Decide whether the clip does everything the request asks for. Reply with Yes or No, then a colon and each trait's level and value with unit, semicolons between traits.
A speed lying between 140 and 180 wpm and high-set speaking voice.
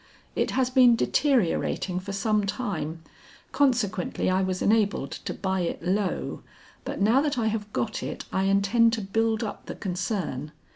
Yes: average, 160 wpm; high, 205 Hz